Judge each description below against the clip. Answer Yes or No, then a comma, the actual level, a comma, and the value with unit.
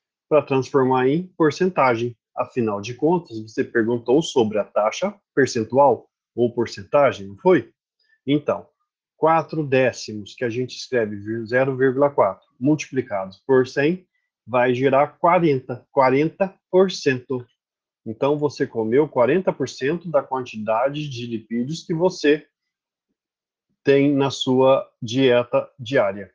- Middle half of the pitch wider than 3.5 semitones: Yes, average, 4.0 semitones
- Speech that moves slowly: Yes, slow, 105 wpm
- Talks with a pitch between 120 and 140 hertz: Yes, low, 135 Hz